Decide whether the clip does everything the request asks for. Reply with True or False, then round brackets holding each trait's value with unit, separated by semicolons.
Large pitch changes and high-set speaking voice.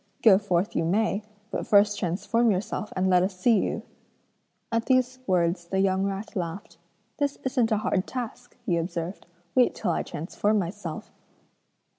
False (3.7 semitones; 195 Hz)